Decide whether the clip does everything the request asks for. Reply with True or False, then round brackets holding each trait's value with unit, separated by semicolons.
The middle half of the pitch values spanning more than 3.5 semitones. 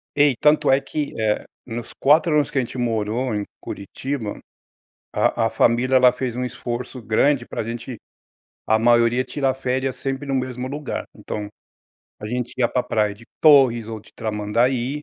False (2.8 semitones)